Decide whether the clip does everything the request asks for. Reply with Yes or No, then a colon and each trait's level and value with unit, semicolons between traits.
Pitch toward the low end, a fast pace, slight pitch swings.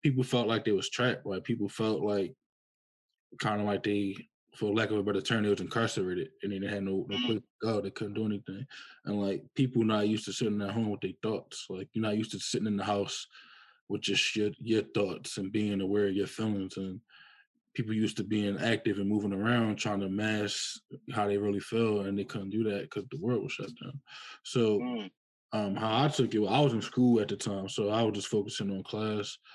Yes: low, 105 Hz; fast, 235 wpm; narrow, 2.0 semitones